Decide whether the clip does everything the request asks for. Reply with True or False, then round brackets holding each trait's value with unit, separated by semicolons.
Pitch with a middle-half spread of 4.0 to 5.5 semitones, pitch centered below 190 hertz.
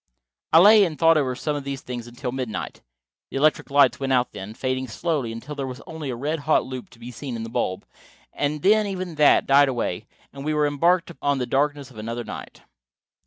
False (3.5 semitones; 140 Hz)